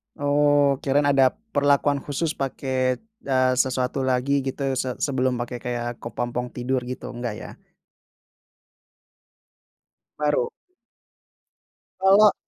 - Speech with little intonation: Yes, narrow, 2.2 semitones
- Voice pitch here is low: Yes, low, 130 Hz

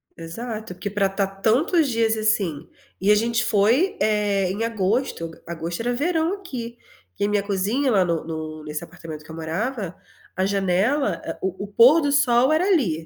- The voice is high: Yes, high, 210 Hz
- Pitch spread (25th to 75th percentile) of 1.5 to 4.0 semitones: No, average, 5.2 semitones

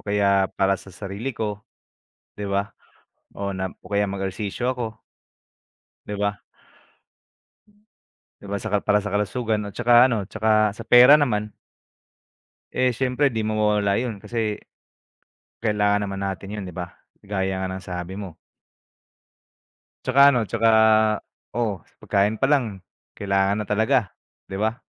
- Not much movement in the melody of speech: Yes, narrow, 2.3 semitones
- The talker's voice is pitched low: Yes, low, 105 Hz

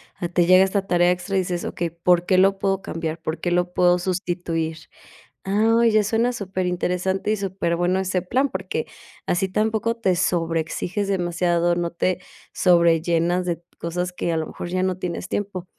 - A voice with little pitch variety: Yes, narrow, 1.8 semitones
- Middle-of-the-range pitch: Yes, medium, 180 Hz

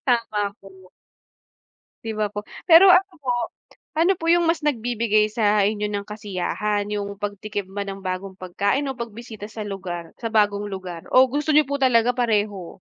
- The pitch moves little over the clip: No, average, 3.3 semitones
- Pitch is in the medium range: No, high, 210 Hz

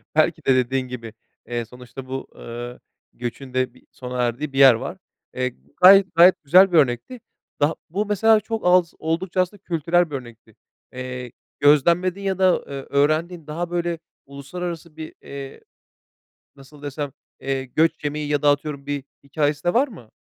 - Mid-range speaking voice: Yes, medium, 145 Hz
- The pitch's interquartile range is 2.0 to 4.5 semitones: No, average, 5.1 semitones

